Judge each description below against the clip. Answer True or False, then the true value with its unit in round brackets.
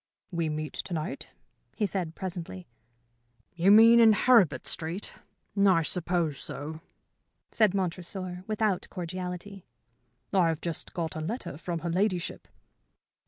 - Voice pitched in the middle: True (180 Hz)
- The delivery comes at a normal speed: False (125 wpm)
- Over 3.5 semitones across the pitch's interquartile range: False (3.2 semitones)